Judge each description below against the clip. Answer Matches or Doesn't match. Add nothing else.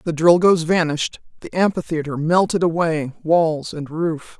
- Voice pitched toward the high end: Doesn't match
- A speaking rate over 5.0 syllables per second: Doesn't match